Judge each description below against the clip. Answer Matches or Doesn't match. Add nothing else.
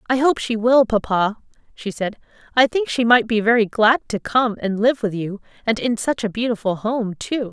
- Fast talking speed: Matches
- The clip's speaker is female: Matches